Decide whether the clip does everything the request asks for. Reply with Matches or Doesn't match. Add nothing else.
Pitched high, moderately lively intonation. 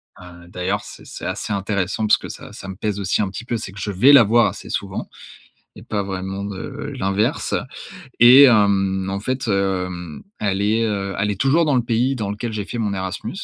Doesn't match